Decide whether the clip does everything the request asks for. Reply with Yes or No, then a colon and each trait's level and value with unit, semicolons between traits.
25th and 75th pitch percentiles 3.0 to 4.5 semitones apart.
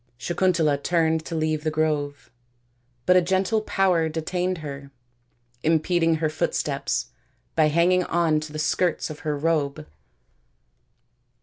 No: narrow, 2.4 semitones